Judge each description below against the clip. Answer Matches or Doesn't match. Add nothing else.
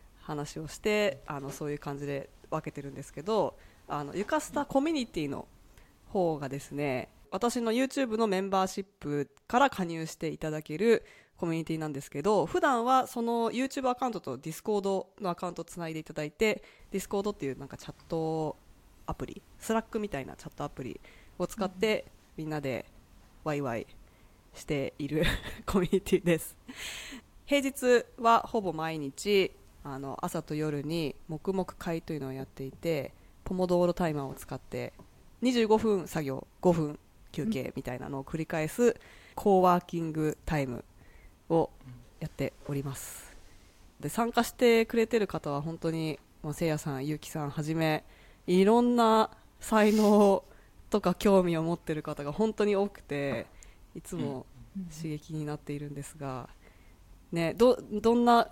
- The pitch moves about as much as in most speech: Doesn't match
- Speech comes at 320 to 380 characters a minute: Matches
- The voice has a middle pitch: Matches